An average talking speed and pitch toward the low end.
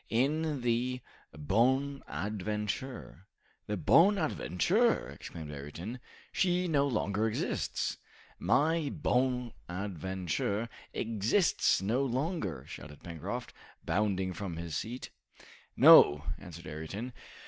No: slow, 85 wpm; low, 110 Hz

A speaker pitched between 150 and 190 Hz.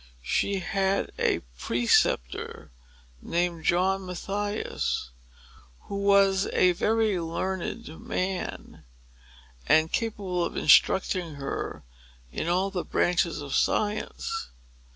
Yes: medium, 185 Hz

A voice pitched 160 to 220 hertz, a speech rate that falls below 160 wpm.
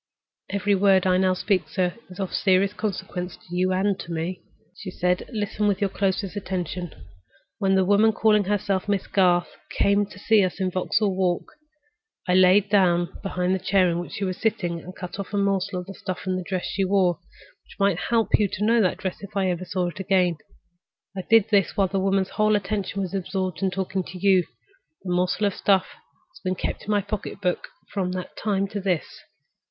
No: high, 190 Hz; fast, 205 wpm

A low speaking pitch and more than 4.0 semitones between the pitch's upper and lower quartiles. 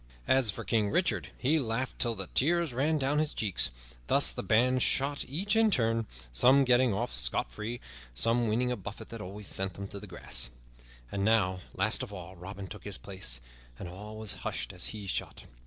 Yes: low, 110 Hz; average, 5.1 semitones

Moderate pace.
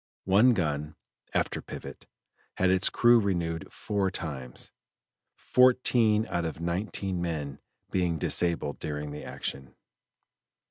No: slow, 110 wpm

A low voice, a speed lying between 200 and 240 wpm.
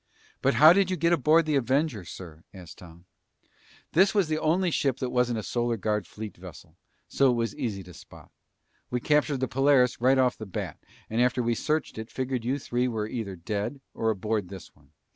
Yes: low, 125 Hz; fast, 205 wpm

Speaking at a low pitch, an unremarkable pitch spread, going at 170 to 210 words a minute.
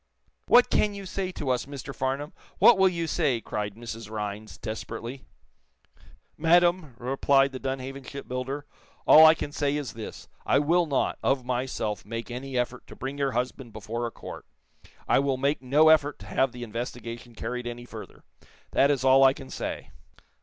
Yes: low, 130 Hz; average, 3.3 semitones; average, 175 wpm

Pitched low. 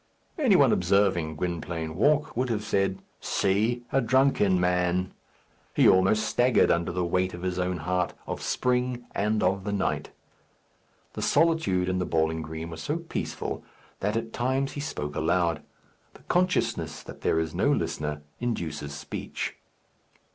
Yes: very low, 95 Hz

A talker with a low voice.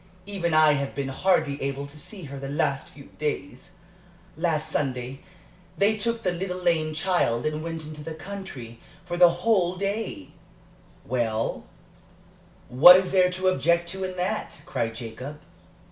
No: medium, 160 Hz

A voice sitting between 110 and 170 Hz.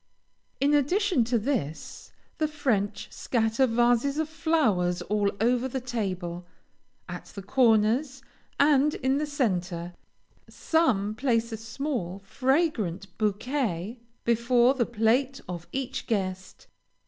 No: high, 235 Hz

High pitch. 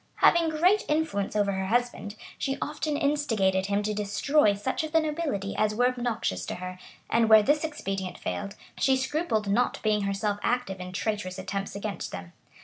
Yes: high, 215 Hz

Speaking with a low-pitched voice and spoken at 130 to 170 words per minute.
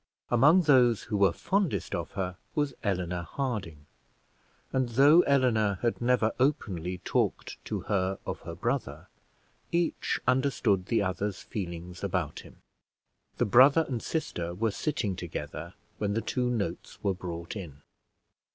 Yes: low, 105 Hz; average, 140 wpm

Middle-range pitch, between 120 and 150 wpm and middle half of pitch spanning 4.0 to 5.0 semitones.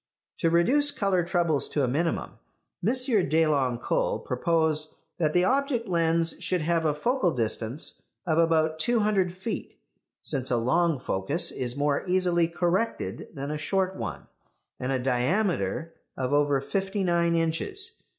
Yes: medium, 165 Hz; average, 145 wpm; average, 4.4 semitones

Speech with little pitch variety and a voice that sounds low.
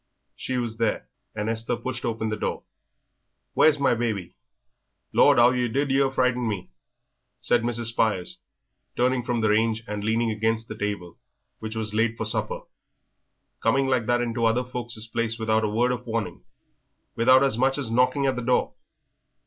Yes: narrow, 2.0 semitones; low, 115 Hz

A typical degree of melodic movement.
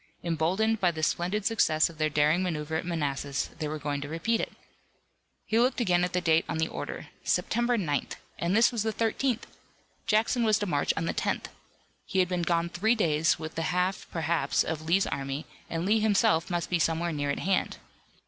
Yes: average, 4.6 semitones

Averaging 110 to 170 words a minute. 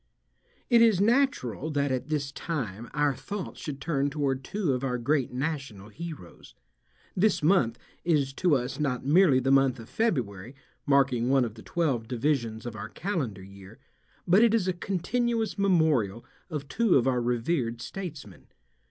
Yes: average, 160 wpm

